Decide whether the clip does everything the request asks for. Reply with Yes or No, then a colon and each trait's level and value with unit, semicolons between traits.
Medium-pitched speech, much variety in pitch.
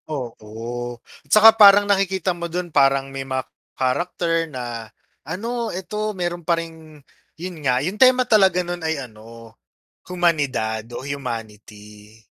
Yes: medium, 160 Hz; wide, 7.0 semitones